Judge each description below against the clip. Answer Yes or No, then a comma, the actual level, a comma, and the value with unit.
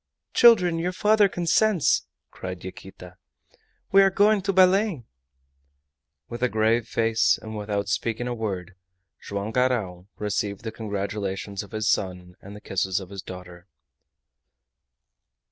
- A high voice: No, low, 110 Hz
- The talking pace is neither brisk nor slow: No, slow, 130 wpm